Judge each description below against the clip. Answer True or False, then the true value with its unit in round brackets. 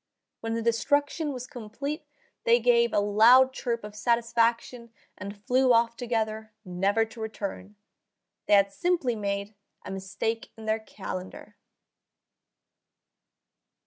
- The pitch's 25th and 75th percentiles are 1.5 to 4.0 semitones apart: True (3.1 semitones)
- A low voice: False (225 Hz)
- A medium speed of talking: False (120 wpm)